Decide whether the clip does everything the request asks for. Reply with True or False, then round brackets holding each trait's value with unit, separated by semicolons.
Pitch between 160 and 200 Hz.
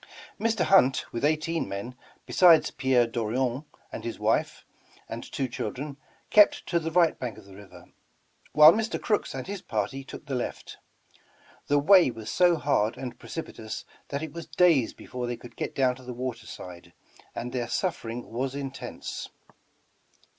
False (130 Hz)